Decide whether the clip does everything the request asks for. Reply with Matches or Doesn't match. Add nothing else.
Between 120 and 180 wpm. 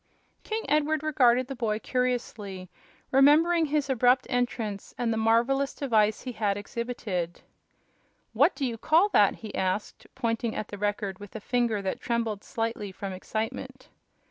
Matches